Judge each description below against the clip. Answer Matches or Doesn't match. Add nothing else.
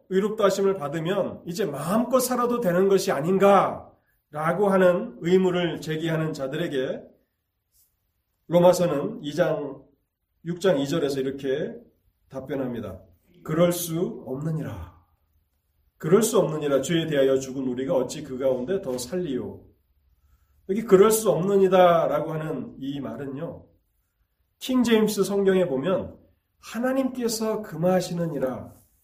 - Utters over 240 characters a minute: Matches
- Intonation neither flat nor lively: Doesn't match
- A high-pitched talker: Doesn't match